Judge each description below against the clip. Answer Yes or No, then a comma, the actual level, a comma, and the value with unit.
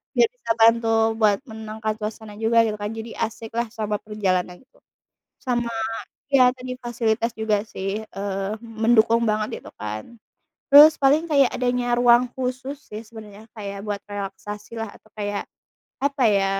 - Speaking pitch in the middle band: No, high, 220 Hz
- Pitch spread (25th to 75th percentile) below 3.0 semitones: Yes, narrow, 2.6 semitones